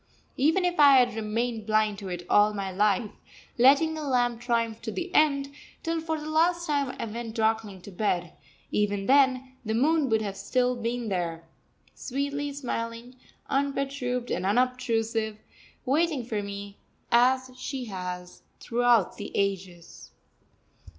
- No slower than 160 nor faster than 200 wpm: No, average, 145 wpm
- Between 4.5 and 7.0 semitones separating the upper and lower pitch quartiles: Yes, average, 4.8 semitones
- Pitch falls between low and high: No, high, 235 Hz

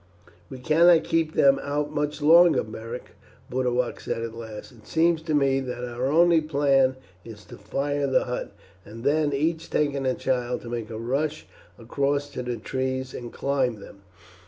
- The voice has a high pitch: No, low, 135 Hz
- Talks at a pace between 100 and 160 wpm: No, average, 175 wpm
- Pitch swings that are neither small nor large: Yes, average, 3.4 semitones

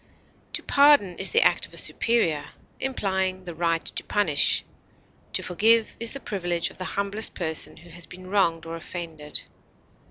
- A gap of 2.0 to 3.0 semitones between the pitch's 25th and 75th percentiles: No, average, 3.8 semitones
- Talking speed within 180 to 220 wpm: No, average, 165 wpm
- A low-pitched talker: No, medium, 185 Hz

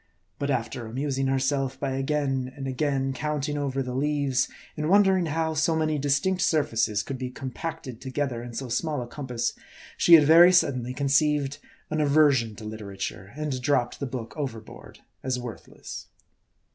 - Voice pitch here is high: No, low, 135 Hz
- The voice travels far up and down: No, average, 3.0 semitones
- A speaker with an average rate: Yes, average, 160 wpm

